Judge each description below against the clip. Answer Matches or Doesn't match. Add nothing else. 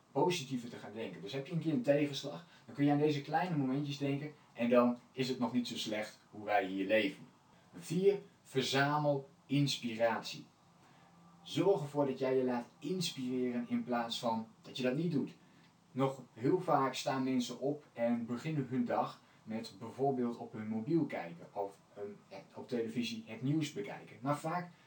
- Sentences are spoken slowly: Doesn't match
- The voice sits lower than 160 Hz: Matches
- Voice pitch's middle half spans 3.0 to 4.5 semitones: Matches